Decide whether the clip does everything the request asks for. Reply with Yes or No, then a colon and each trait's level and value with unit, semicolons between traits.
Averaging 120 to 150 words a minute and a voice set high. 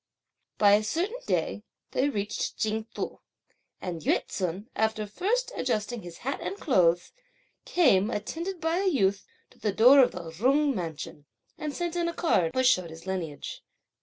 No: average, 165 wpm; high, 220 Hz